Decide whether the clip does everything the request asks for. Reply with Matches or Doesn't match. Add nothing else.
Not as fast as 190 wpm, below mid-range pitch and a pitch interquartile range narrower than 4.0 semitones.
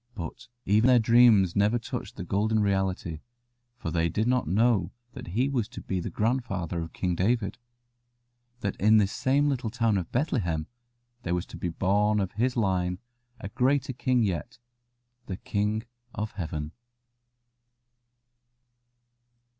Doesn't match